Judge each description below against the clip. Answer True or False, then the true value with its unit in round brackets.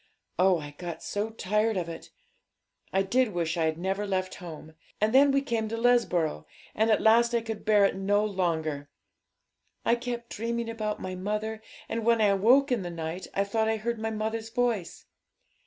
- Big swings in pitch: False (3.7 semitones)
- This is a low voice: False (215 Hz)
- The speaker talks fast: False (190 wpm)